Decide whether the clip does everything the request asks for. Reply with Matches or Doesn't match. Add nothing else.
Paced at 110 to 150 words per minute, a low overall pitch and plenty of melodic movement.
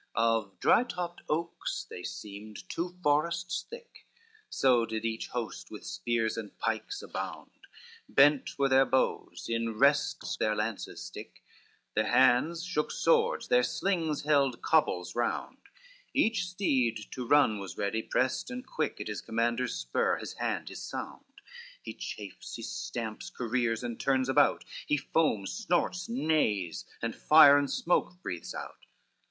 Matches